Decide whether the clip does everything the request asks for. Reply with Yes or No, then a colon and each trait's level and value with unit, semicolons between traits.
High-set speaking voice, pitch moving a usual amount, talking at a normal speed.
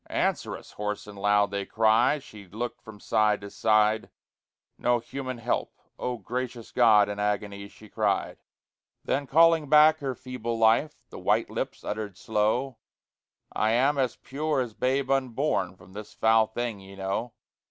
No: low, 110 Hz; average, 3.8 semitones; average, 160 wpm